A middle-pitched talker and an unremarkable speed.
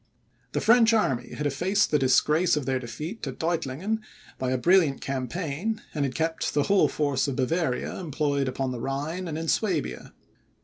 Yes: medium, 150 Hz; average, 175 wpm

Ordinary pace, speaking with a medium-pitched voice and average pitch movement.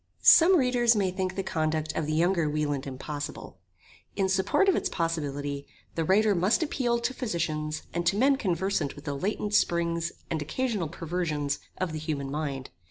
Yes: average, 170 wpm; medium, 170 Hz; average, 4.9 semitones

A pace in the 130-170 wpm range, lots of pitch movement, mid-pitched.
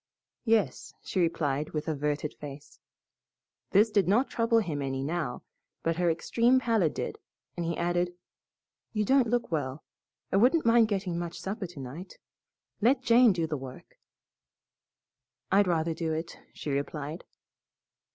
Yes: average, 140 wpm; wide, 6.3 semitones; medium, 175 Hz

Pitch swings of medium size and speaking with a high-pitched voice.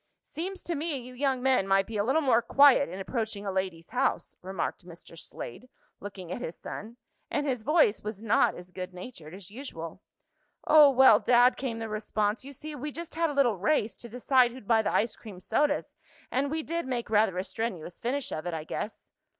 No: wide, 5.9 semitones; high, 235 Hz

